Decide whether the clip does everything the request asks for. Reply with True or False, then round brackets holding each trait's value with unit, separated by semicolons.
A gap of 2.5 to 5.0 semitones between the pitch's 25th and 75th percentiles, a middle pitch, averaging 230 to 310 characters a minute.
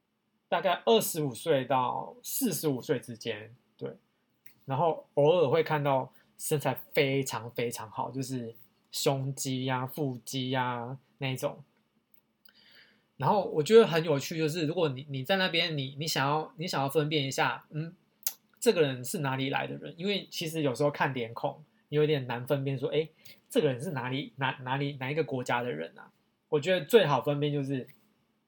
True (3.4 semitones; 145 Hz; 260 characters per minute)